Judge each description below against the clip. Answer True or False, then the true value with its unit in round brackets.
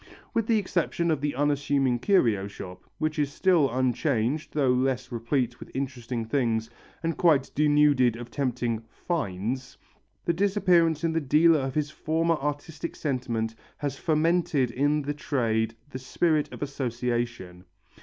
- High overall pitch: False (140 Hz)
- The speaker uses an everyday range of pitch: True (4.3 semitones)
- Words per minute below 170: True (145 wpm)